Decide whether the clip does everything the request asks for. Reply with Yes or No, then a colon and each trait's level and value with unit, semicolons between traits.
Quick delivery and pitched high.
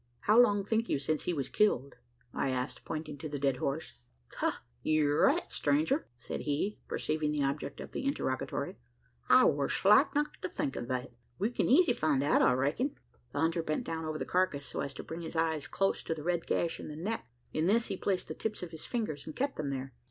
No: fast, 225 wpm; medium, 155 Hz